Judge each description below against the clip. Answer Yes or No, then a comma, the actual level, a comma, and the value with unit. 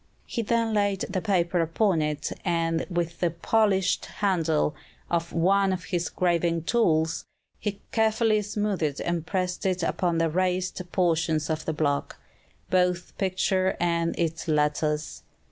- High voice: No, medium, 175 Hz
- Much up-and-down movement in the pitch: No, average, 2.7 semitones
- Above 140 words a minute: No, slow, 135 wpm